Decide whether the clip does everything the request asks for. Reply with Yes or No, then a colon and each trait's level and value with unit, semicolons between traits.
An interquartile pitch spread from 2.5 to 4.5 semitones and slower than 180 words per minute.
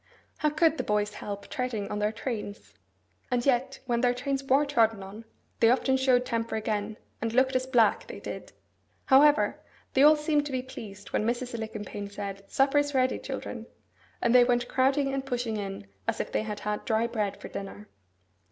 No: average, 4.0 semitones; average, 190 wpm